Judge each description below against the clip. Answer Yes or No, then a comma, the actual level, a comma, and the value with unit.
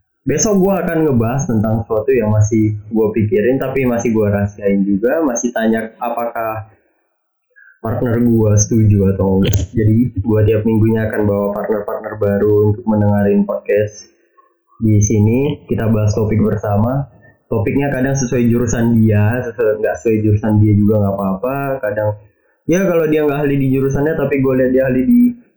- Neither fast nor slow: No, fast, 155 wpm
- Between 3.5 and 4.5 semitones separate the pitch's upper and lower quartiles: Yes, average, 3.8 semitones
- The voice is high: No, low, 110 Hz